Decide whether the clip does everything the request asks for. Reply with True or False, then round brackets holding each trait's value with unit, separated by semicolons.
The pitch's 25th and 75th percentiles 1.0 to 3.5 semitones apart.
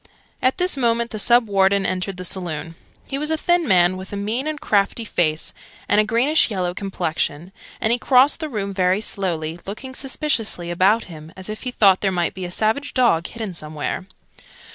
False (5.0 semitones)